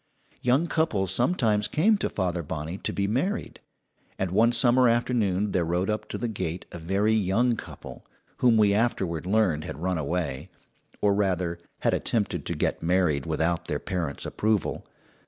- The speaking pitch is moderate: No, low, 100 Hz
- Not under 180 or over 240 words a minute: No, average, 165 wpm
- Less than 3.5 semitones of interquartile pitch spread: No, average, 4.9 semitones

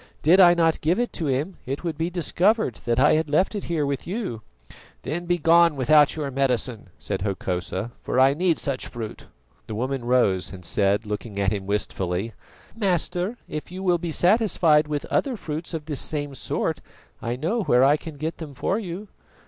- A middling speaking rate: Yes, average, 190 wpm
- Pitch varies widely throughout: Yes, wide, 6.2 semitones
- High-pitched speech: No, medium, 150 Hz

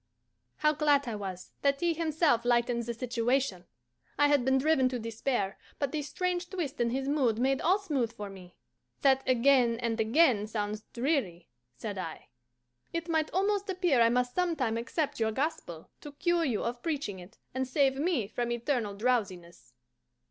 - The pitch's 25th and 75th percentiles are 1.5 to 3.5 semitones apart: No, average, 5.0 semitones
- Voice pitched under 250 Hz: No, very high, 255 Hz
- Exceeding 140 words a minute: Yes, average, 170 wpm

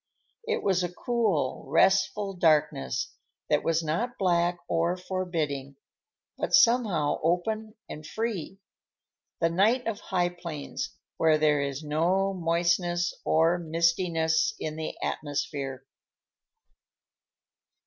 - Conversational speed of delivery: No, slow, 105 wpm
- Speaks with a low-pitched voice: No, medium, 170 Hz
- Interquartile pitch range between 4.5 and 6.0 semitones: No, average, 3.5 semitones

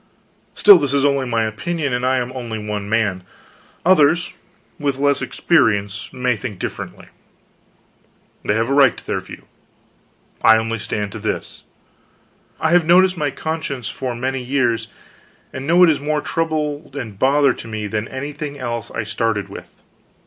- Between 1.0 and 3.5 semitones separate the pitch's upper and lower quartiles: No, average, 4.6 semitones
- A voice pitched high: No, low, 130 Hz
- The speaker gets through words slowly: No, average, 165 wpm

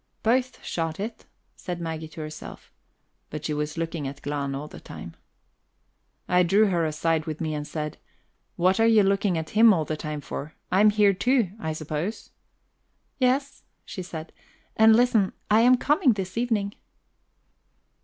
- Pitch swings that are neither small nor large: No, wide, 5.8 semitones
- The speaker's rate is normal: Yes, average, 165 wpm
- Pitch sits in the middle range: Yes, medium, 180 Hz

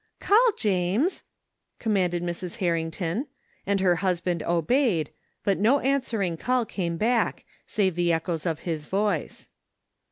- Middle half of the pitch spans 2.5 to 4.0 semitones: No, average, 4.7 semitones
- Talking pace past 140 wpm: No, slow, 135 wpm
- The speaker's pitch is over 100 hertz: Yes, medium, 185 Hz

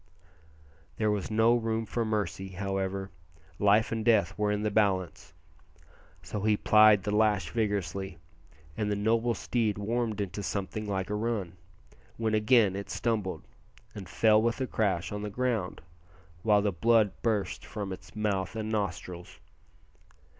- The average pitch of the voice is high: No, low, 105 Hz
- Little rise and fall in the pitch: Yes, narrow, 2.2 semitones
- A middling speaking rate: Yes, average, 150 wpm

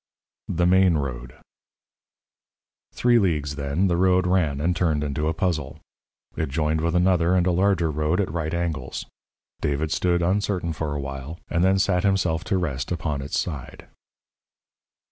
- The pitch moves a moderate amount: Yes, average, 3.5 semitones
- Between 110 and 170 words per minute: Yes, average, 160 wpm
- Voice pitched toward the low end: Yes, very low, 85 Hz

